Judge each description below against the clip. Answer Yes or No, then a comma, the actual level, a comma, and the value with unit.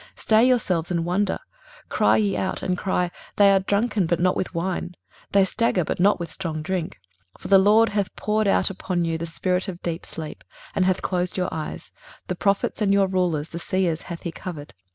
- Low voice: No, medium, 185 Hz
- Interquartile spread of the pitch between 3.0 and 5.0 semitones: No, narrow, 2.5 semitones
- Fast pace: Yes, fast, 215 wpm